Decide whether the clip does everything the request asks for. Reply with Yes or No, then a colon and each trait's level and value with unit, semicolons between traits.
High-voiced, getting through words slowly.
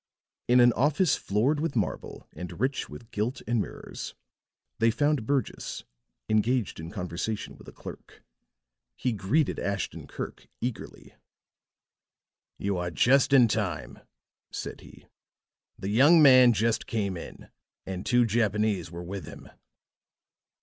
No: low, 115 Hz; slow, 130 wpm